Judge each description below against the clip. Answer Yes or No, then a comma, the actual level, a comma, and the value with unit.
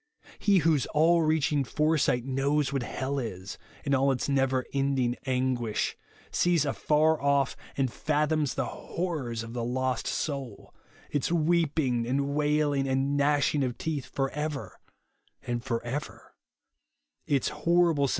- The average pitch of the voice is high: No, medium, 140 Hz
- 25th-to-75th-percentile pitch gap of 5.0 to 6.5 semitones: No, average, 2.7 semitones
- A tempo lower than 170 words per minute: Yes, average, 140 wpm